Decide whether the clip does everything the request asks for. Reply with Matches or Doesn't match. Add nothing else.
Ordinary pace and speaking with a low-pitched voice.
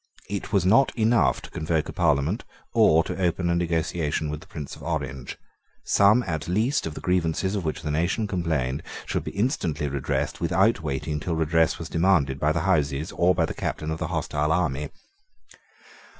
Matches